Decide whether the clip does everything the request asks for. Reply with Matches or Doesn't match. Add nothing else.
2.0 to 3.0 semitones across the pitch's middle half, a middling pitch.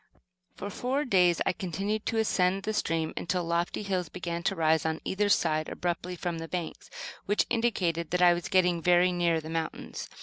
Matches